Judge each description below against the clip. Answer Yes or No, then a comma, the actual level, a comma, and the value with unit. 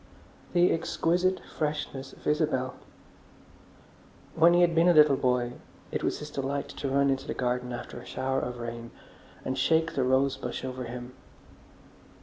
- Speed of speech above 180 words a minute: No, average, 160 wpm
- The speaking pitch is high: No, low, 135 Hz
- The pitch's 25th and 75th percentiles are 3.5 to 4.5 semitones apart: Yes, average, 3.8 semitones